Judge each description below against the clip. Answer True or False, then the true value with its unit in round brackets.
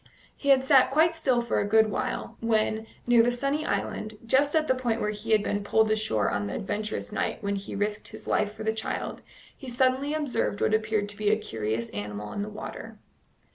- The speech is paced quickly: True (215 wpm)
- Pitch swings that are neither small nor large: True (3.8 semitones)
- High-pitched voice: True (220 Hz)